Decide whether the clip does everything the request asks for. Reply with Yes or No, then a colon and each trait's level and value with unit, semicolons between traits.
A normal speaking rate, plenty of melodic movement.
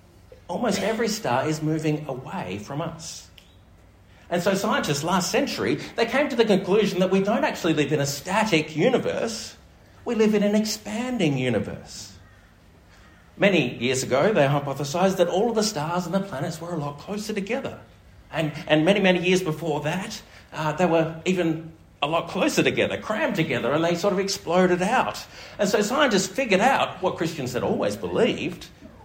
Yes: average, 175 wpm; wide, 6.2 semitones